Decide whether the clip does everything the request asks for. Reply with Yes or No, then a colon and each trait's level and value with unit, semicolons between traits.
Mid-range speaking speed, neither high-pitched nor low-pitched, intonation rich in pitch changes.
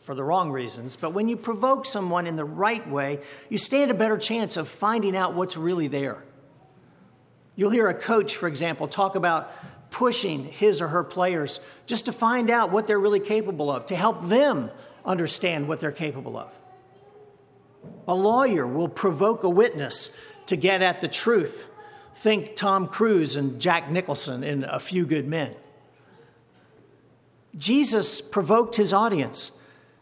No: average, 160 wpm; high, 195 Hz; wide, 5.8 semitones